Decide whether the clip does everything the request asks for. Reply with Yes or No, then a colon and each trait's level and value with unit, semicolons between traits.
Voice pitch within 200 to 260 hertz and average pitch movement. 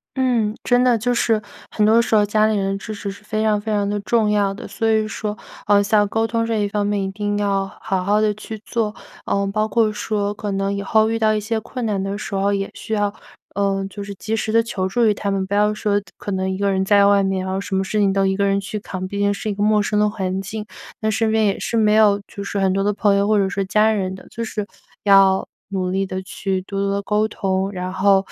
No: high, 205 Hz; narrow, 1.6 semitones